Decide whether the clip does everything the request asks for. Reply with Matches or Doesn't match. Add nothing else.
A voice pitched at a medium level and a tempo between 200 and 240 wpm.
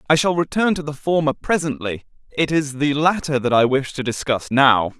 Matches